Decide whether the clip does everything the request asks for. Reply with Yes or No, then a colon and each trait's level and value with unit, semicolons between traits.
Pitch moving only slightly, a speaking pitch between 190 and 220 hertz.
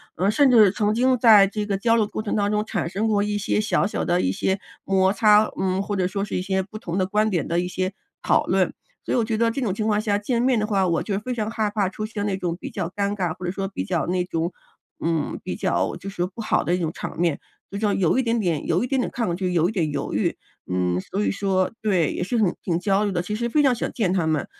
No: average, 3.1 semitones; high, 200 Hz